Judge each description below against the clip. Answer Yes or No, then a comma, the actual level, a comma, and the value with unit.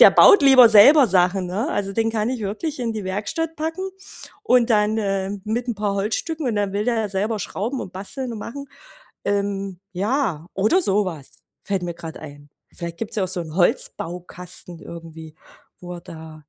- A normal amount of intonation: Yes, average, 4.6 semitones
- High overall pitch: Yes, high, 205 Hz